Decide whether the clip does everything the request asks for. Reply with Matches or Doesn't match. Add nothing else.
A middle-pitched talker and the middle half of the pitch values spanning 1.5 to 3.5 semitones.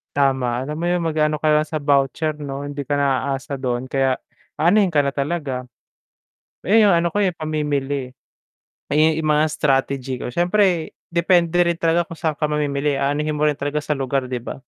Matches